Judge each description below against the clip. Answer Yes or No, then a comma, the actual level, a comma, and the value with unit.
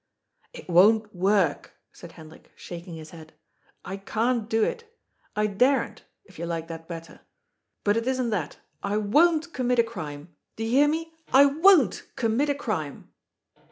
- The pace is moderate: Yes, average, 170 wpm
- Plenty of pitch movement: Yes, wide, 7.4 semitones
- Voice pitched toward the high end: Yes, high, 215 Hz